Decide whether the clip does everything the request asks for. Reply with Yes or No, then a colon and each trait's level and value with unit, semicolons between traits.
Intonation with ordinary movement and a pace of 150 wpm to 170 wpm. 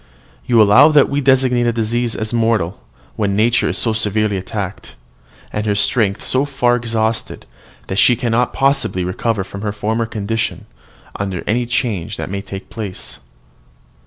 Yes: average, 3.0 semitones; average, 155 wpm